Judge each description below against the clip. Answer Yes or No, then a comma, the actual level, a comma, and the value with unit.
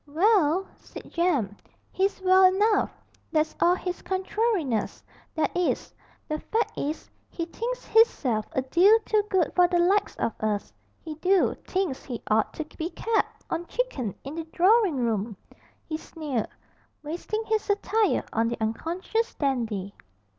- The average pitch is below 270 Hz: No, very high, 340 Hz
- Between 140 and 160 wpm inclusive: Yes, average, 145 wpm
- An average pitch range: No, wide, 6.8 semitones